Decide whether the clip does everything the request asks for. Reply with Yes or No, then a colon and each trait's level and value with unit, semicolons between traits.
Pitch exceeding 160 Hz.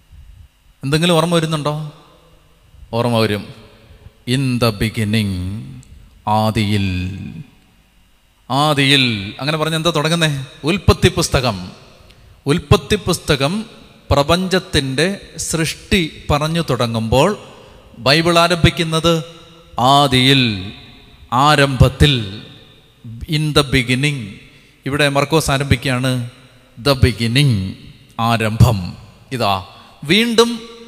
No: low, 135 Hz